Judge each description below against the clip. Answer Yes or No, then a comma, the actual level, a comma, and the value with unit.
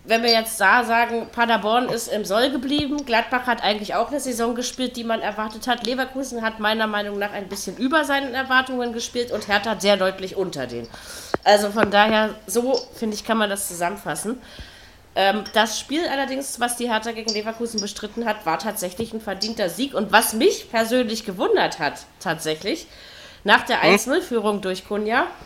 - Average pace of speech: Yes, average, 180 wpm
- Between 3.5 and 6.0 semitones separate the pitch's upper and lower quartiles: No, average, 2.9 semitones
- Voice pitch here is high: Yes, high, 225 Hz